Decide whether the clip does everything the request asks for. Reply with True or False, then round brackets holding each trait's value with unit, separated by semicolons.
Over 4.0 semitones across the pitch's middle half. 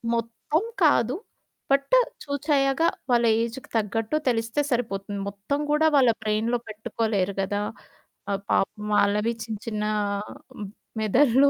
True (4.4 semitones)